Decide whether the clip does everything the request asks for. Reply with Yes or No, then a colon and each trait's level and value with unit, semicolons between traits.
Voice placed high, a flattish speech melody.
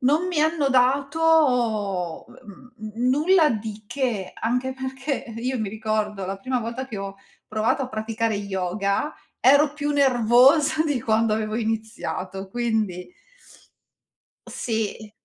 No: high, 235 Hz; average, 4.0 semitones